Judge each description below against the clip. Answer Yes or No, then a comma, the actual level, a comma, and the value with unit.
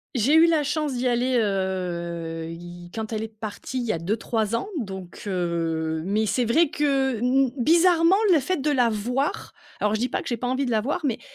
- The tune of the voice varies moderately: No, wide, 6.2 semitones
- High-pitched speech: Yes, high, 230 Hz